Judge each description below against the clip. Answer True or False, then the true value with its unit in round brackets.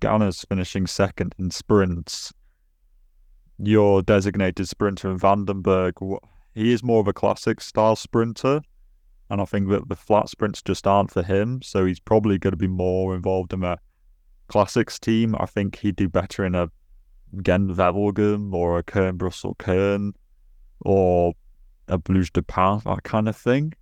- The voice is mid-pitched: False (95 Hz)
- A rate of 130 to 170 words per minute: True (160 wpm)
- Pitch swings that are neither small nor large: False (2.3 semitones)